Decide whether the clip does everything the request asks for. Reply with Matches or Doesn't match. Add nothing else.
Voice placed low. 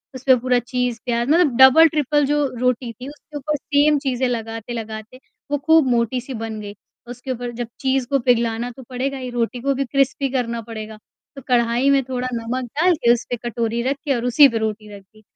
Doesn't match